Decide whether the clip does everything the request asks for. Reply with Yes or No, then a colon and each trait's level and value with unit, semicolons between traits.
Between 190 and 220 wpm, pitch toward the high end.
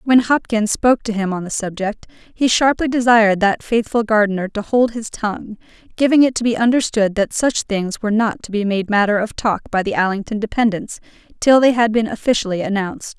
Yes: average, 200 wpm; high, 220 Hz